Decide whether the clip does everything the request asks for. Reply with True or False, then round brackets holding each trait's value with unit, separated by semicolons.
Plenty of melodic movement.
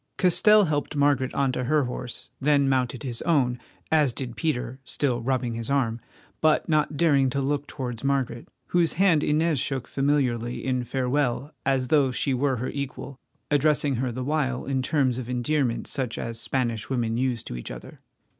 False (2.9 semitones)